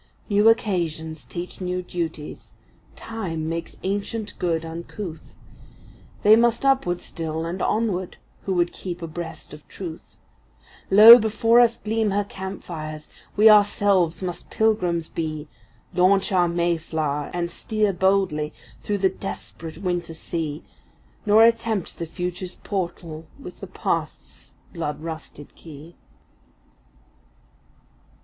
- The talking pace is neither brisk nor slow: No, slow, 120 wpm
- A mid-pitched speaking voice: Yes, medium, 180 Hz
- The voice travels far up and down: No, average, 4.0 semitones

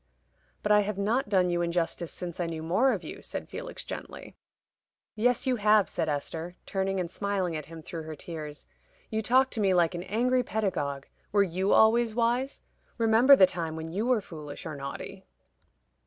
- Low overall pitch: No, high, 190 Hz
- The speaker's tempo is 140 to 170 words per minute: No, average, 185 wpm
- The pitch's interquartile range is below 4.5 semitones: No, average, 5.0 semitones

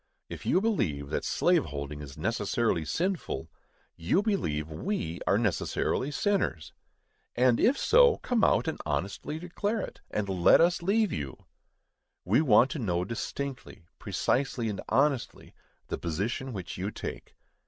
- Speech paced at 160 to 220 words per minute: No, average, 145 wpm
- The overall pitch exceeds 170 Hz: No, low, 120 Hz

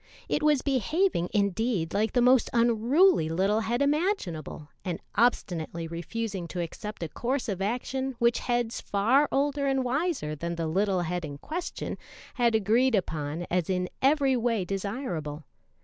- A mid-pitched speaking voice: No, high, 220 Hz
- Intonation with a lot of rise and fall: Yes, wide, 6.9 semitones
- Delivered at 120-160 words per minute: Yes, average, 150 wpm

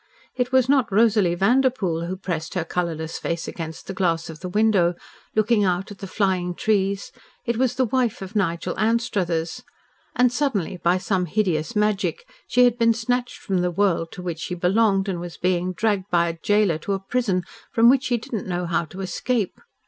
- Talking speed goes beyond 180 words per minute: Yes, average, 195 wpm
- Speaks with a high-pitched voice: Yes, high, 195 Hz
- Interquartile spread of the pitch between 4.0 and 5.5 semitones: Yes, average, 4.5 semitones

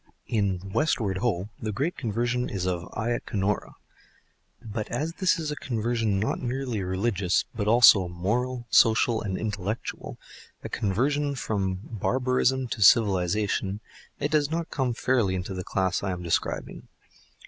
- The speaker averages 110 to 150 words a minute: Yes, average, 140 wpm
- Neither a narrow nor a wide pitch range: Yes, average, 4.5 semitones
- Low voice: Yes, low, 110 Hz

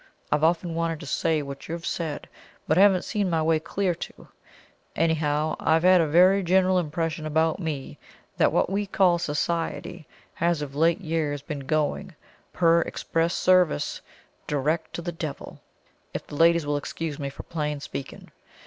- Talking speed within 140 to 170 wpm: Yes, average, 165 wpm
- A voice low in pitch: No, medium, 165 Hz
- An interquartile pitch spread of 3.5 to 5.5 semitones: No, narrow, 2.4 semitones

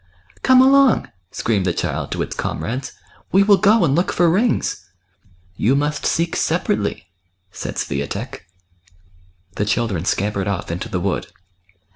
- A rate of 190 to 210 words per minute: No, average, 160 wpm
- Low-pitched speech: Yes, low, 120 Hz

